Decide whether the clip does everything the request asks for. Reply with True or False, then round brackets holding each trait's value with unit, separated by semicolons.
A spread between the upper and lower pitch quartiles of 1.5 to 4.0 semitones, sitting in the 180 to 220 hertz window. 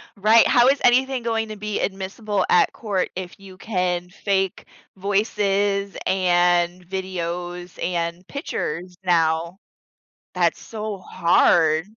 True (2.9 semitones; 190 Hz)